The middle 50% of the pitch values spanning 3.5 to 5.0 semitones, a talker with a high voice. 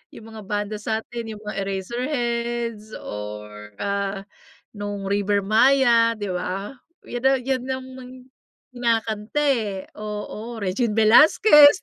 No: average, 3.0 semitones; high, 220 Hz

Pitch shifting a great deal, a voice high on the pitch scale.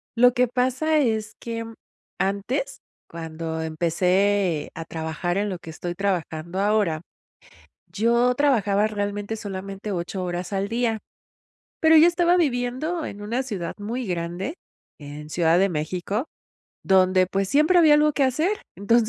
Yes: wide, 5.9 semitones; high, 205 Hz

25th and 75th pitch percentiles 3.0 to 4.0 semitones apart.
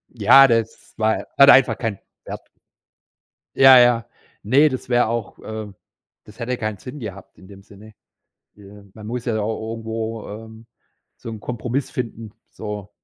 No: narrow, 2.4 semitones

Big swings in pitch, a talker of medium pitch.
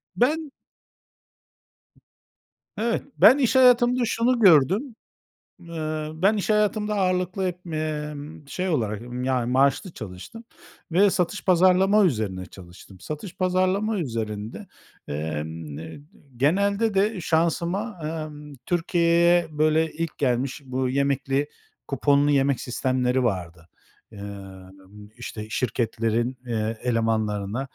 Yes: wide, 8.3 semitones; medium, 150 Hz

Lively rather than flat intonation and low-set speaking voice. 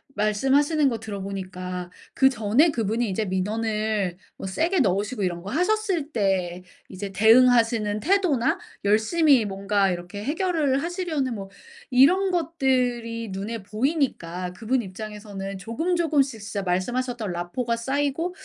No: wide, 5.9 semitones; high, 225 Hz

